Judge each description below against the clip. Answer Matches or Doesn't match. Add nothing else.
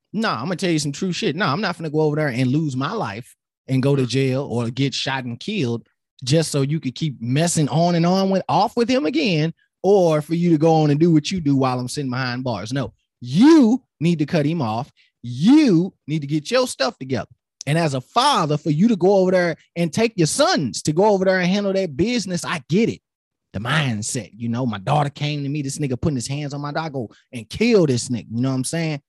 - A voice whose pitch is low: Doesn't match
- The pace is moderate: Doesn't match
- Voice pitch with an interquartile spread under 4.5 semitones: Doesn't match